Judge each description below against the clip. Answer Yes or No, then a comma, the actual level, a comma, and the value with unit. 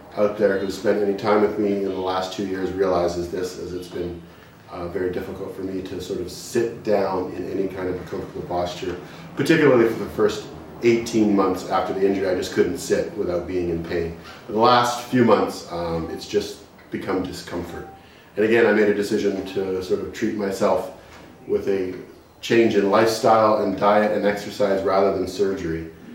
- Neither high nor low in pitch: No, very low, 95 Hz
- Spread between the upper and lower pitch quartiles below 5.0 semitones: Yes, average, 2.8 semitones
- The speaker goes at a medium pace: Yes, average, 195 wpm